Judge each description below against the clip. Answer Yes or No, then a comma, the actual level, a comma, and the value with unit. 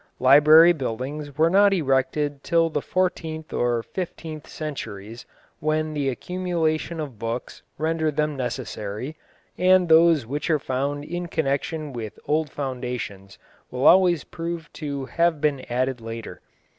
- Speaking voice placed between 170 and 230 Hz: No, medium, 150 Hz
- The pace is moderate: No, slow, 130 wpm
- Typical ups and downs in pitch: Yes, average, 4.0 semitones